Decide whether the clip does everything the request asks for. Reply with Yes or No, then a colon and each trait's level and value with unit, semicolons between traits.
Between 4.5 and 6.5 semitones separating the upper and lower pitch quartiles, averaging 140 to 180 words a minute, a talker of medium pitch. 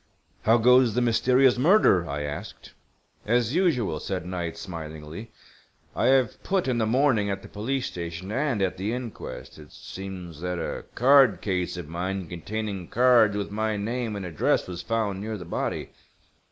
No: average, 5.3 semitones; average, 165 wpm; low, 105 Hz